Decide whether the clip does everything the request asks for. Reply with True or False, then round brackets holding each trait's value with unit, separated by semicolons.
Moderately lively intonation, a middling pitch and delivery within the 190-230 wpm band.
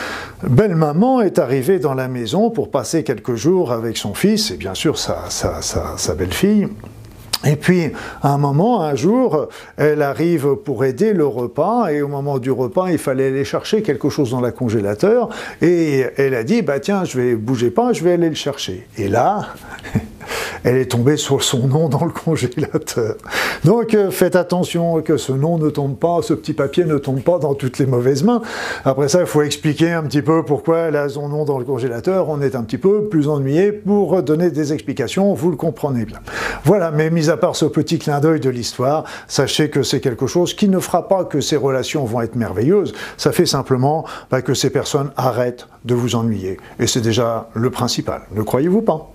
True (4.4 semitones; 150 Hz; 210 wpm)